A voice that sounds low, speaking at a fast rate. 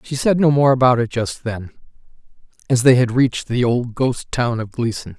Yes: low, 125 Hz; fast, 210 wpm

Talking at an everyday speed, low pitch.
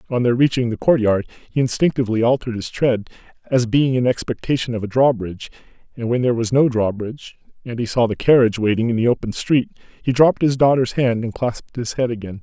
No: fast, 210 wpm; low, 120 Hz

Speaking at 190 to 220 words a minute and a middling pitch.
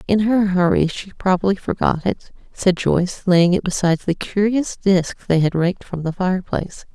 No: average, 180 wpm; medium, 175 Hz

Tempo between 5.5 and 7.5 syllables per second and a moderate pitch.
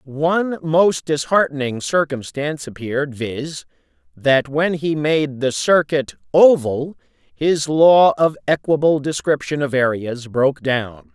No: 3.9 syllables/s; medium, 150 Hz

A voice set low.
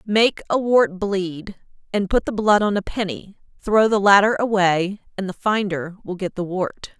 No: high, 195 Hz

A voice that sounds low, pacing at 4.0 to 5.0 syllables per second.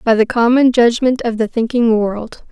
No: high, 235 Hz; 4.7 syllables/s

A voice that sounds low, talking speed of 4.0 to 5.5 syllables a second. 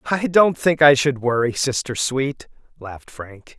Yes: low, 130 Hz; 4.3 syllables/s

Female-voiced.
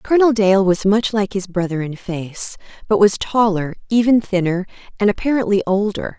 Yes: female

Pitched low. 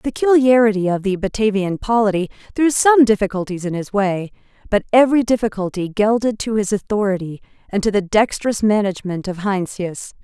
No: high, 210 Hz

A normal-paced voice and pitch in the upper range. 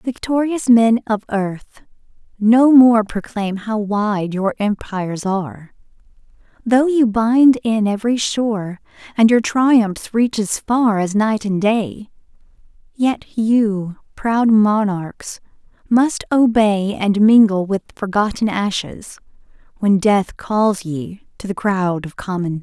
No: slow, 130 wpm; high, 215 Hz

